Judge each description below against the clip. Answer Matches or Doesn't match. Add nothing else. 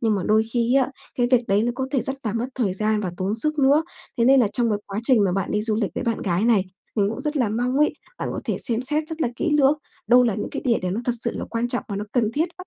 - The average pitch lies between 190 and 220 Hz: Doesn't match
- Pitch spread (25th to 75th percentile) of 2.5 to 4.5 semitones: Matches